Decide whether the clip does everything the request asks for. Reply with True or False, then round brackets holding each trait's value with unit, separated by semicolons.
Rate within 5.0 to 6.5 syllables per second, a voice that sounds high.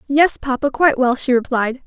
True (5.4 syllables/s; 265 Hz)